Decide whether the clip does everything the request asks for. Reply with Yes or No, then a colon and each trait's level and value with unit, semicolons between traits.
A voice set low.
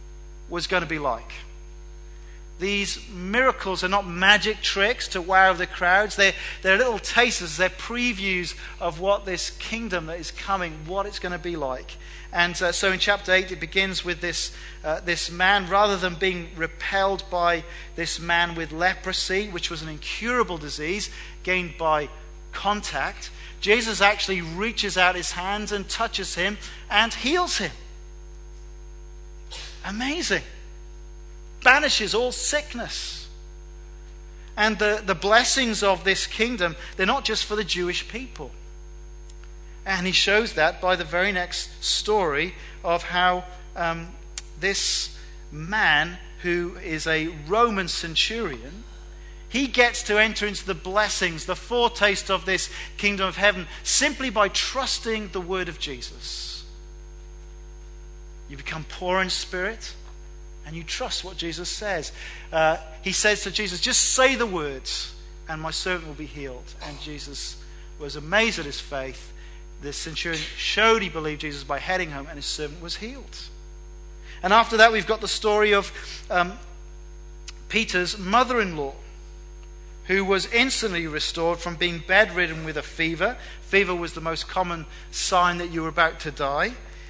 No: medium, 180 Hz